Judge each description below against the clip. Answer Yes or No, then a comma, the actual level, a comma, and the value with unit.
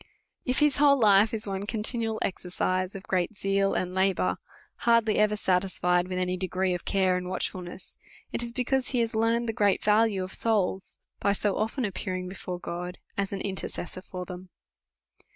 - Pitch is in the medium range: No, high, 195 Hz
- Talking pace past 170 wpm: Yes, average, 180 wpm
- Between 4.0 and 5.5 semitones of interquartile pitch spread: No, average, 3.3 semitones